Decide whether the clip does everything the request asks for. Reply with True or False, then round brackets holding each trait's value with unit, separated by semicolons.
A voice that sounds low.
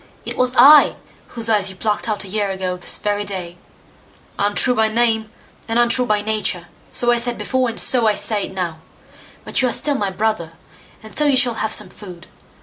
False (220 Hz)